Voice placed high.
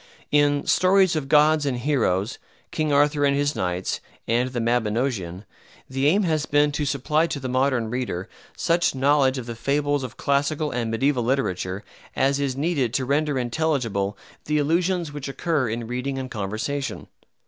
No: medium, 140 Hz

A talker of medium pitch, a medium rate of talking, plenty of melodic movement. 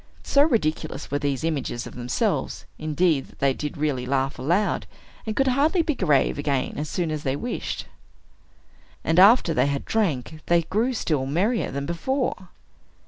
Yes: medium, 155 Hz; average, 165 wpm; wide, 7.1 semitones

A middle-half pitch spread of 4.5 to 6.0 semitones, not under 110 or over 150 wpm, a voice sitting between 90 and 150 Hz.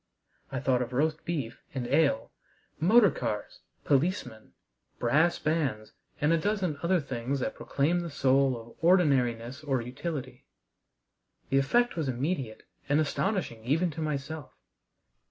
Yes: average, 4.8 semitones; slow, 135 wpm; medium, 140 Hz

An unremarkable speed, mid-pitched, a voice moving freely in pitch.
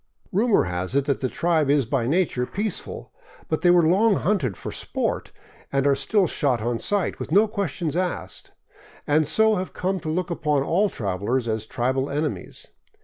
Yes: average, 180 wpm; medium, 155 Hz; wide, 6.0 semitones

